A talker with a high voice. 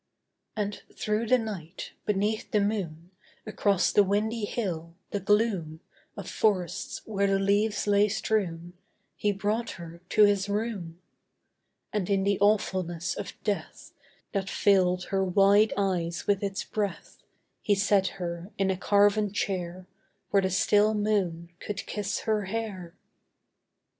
Yes: high, 200 Hz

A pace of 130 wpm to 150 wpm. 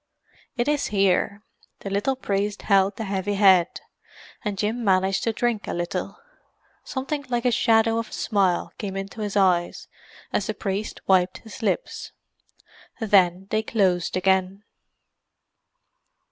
Yes: average, 140 wpm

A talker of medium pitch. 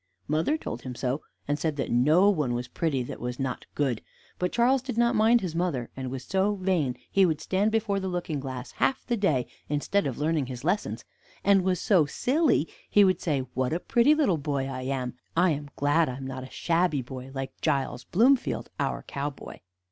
Yes: medium, 155 Hz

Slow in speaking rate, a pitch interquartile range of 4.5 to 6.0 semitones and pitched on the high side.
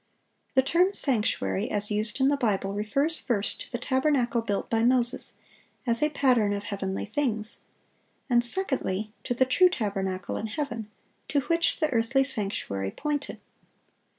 No: average, 150 wpm; average, 4.9 semitones; high, 235 Hz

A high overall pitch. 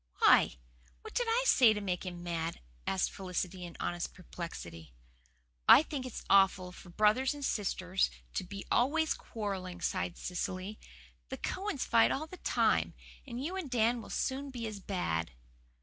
Yes: high, 200 Hz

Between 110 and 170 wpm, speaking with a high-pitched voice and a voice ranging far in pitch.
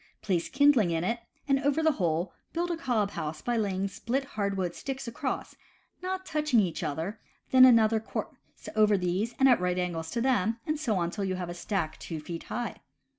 No: average, 200 wpm; high, 215 Hz; wide, 6.6 semitones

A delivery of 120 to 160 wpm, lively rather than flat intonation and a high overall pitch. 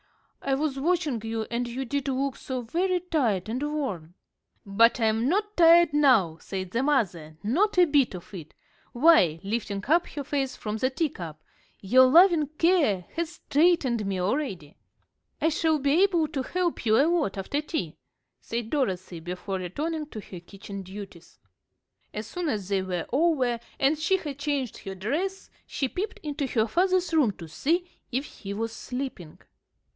No: average, 170 wpm; wide, 7.8 semitones; very high, 260 Hz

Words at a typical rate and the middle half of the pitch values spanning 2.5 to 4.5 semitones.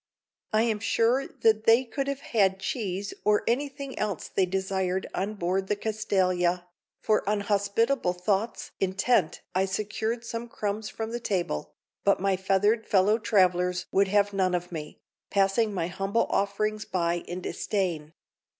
Yes: average, 150 wpm; average, 2.9 semitones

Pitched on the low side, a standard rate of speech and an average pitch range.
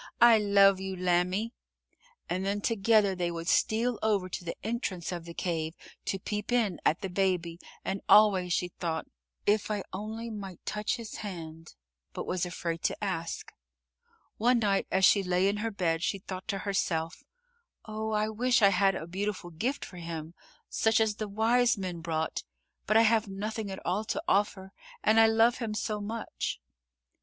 No: high, 195 Hz; average, 180 wpm; average, 3.3 semitones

